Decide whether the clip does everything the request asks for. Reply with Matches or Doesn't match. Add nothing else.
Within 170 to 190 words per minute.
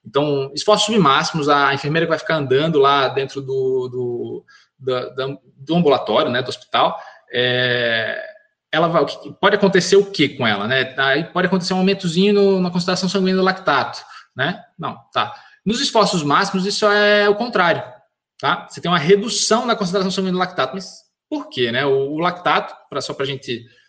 Matches